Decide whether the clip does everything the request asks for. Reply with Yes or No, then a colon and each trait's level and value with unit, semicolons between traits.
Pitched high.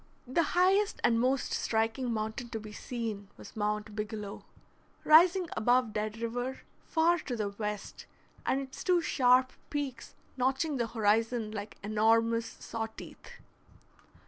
Yes: high, 230 Hz